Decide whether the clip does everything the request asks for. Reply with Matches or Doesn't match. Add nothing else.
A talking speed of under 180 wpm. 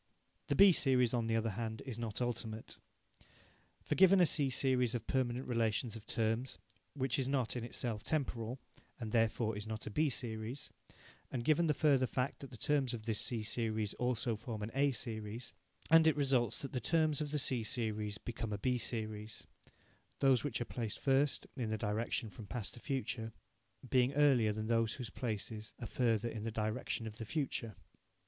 Doesn't match